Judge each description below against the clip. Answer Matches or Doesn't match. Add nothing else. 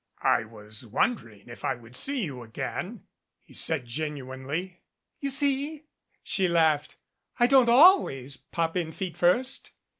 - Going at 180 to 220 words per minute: Doesn't match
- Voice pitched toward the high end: Doesn't match